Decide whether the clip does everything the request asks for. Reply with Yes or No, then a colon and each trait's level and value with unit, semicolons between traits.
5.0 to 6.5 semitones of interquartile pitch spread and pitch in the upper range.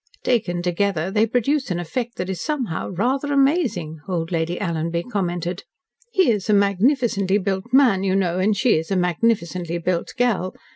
Yes: wide, 5.4 semitones; high, 195 Hz